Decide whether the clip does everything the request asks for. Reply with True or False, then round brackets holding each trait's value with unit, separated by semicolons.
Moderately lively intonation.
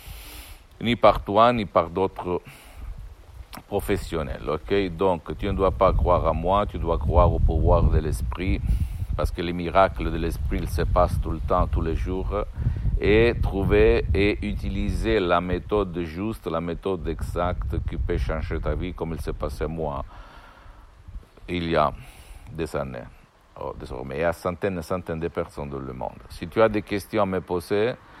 True (3.0 semitones)